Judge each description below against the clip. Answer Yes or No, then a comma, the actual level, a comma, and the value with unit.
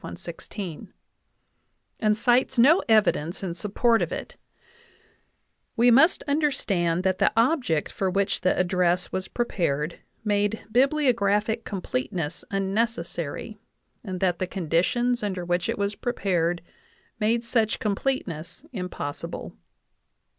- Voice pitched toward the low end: No, high, 200 Hz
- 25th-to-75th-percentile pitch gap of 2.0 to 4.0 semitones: No, average, 4.8 semitones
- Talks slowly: Yes, slow, 120 wpm